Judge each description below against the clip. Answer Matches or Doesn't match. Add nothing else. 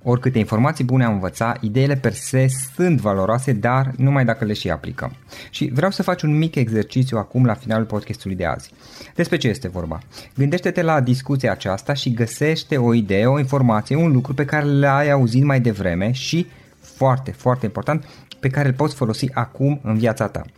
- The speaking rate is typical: Doesn't match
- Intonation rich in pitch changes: Doesn't match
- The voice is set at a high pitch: Doesn't match